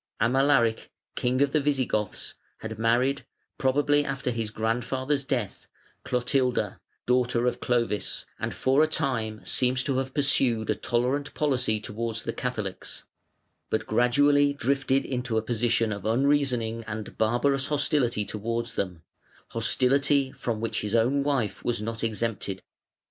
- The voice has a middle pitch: No, low, 125 Hz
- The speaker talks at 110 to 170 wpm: Yes, slow, 135 wpm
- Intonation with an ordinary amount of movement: Yes, average, 3.4 semitones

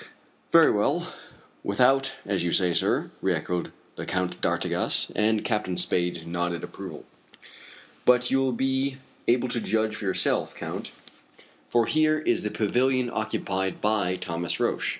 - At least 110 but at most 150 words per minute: Yes, average, 145 wpm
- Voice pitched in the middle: No, low, 110 Hz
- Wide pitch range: Yes, wide, 5.8 semitones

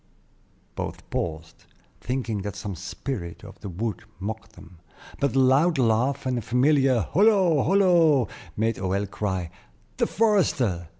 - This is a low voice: Yes, low, 115 Hz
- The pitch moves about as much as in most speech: No, wide, 6.3 semitones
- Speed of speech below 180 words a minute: Yes, slow, 135 wpm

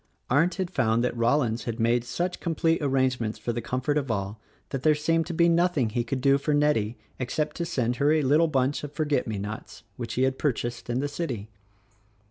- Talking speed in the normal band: No, fast, 220 wpm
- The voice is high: No, low, 130 Hz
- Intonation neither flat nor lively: Yes, average, 4.2 semitones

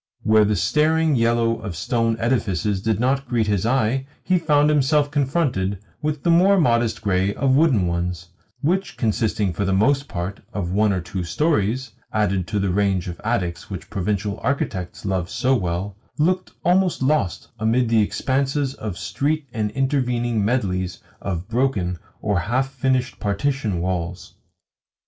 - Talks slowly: No, average, 155 wpm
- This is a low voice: Yes, low, 115 Hz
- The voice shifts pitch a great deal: Yes, wide, 5.8 semitones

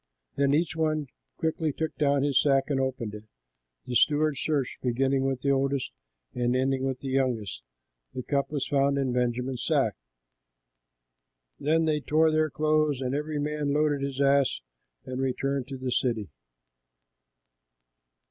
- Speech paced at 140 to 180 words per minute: Yes, average, 155 wpm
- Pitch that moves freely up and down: No, narrow, 2.5 semitones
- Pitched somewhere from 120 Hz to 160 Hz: Yes, medium, 140 Hz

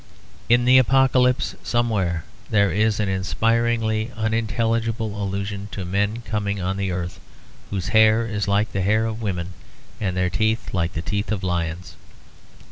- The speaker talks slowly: No, average, 150 wpm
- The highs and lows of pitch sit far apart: No, average, 3.0 semitones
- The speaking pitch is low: Yes, low, 105 Hz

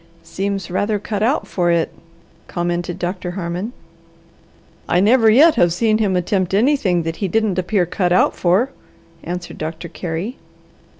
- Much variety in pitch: No, average, 3.6 semitones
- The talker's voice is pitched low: No, medium, 185 Hz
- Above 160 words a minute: No, average, 145 wpm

